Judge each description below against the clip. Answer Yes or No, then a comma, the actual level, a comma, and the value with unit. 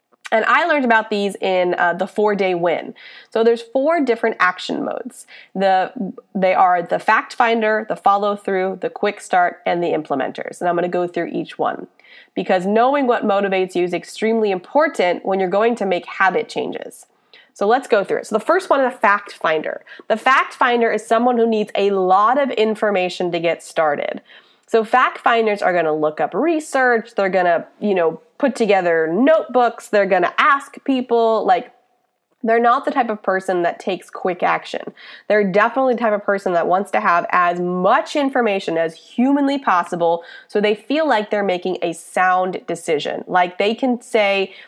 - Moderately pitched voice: No, high, 210 Hz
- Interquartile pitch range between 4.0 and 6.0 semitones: Yes, average, 4.7 semitones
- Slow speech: No, average, 190 wpm